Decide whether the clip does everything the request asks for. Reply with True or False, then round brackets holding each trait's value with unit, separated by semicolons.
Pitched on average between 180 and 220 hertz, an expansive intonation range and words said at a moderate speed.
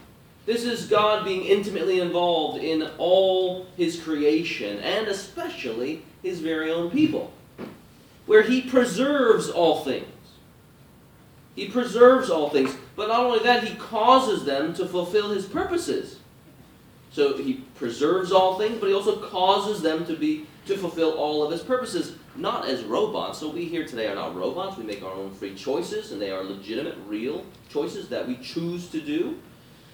True (190 Hz; 7.3 semitones; 160 wpm)